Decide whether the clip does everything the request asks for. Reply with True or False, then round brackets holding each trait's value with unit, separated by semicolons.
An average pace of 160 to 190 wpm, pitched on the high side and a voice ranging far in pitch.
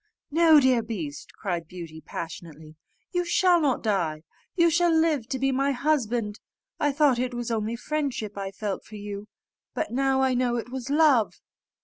True (170 wpm; 245 Hz; 5.8 semitones)